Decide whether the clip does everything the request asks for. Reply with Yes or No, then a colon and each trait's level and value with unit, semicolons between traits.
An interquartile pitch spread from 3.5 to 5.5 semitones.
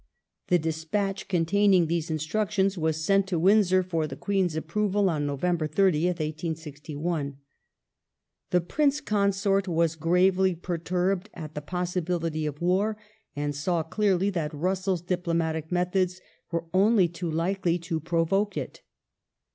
No: average, 3.1 semitones